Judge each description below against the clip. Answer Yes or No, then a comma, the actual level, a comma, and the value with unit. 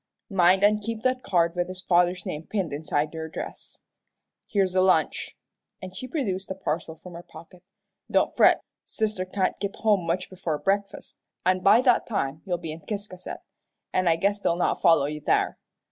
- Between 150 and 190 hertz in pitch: Yes, medium, 185 Hz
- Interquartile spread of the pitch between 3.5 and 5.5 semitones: No, average, 3.1 semitones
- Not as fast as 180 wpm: No, average, 185 wpm